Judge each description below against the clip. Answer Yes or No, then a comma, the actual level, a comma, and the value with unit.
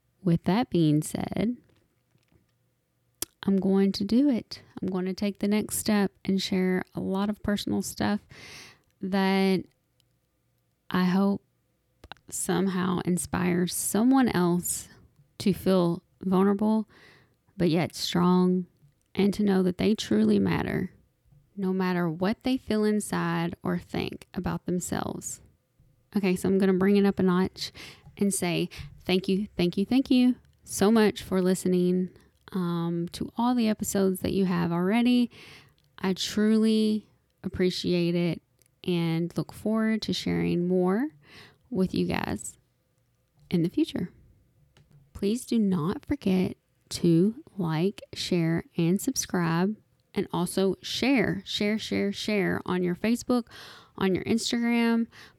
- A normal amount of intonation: Yes, average, 3.2 semitones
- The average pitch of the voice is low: No, high, 190 Hz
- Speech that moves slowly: Yes, slow, 130 wpm